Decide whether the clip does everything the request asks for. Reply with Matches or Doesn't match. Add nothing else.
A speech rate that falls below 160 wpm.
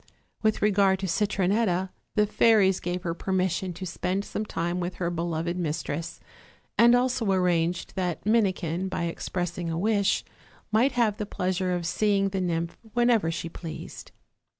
Matches